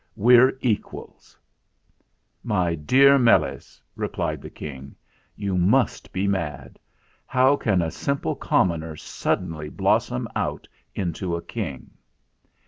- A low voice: Yes, very low, 95 Hz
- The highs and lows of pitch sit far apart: Yes, wide, 6.7 semitones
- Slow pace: Yes, slow, 110 wpm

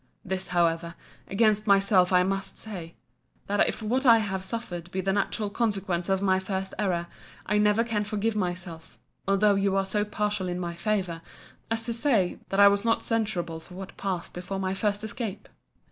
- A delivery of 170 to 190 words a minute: Yes, average, 185 wpm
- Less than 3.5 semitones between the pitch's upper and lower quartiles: Yes, narrow, 2.6 semitones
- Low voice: No, high, 195 Hz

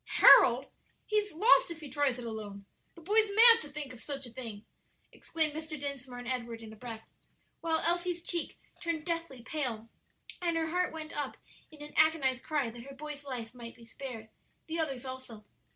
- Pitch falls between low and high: No, very high, 285 Hz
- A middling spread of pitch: Yes, average, 5.0 semitones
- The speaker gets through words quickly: No, average, 190 wpm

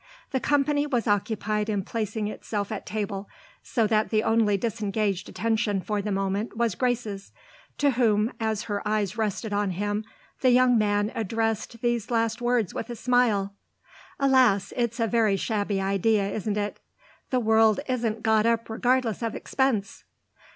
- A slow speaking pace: No, average, 160 wpm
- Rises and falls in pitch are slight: Yes, narrow, 2.3 semitones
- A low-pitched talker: No, high, 220 Hz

